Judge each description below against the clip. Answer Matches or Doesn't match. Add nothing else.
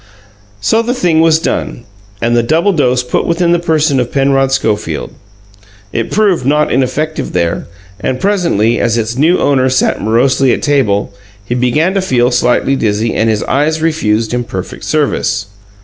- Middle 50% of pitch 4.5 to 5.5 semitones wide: Matches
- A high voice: Doesn't match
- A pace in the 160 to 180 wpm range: Matches